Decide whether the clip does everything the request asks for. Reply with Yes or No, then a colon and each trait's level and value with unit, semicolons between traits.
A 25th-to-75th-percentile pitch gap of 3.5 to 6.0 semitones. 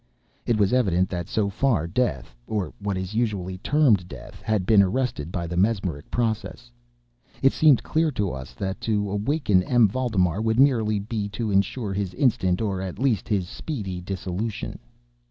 Yes: average, 3.9 semitones